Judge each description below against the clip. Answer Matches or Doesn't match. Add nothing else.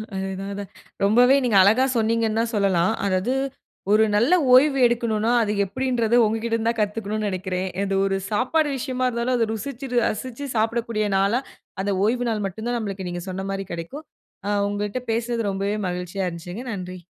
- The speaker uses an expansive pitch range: Doesn't match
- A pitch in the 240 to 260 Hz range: Doesn't match